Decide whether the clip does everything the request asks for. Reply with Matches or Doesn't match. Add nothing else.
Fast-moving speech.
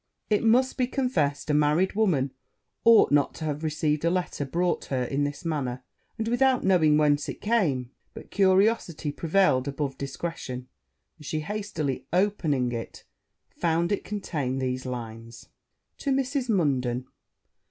Doesn't match